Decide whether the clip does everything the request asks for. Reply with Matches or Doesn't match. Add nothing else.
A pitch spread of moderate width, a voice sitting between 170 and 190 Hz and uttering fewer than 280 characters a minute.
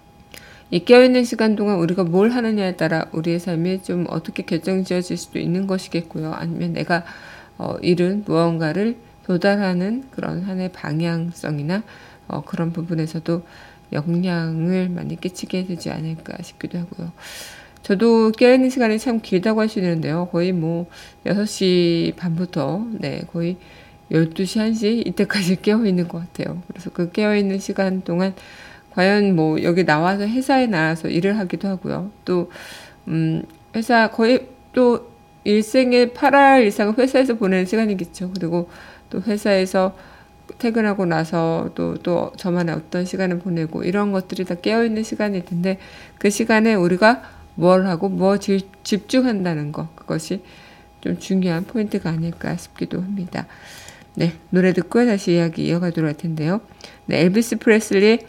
Doesn't match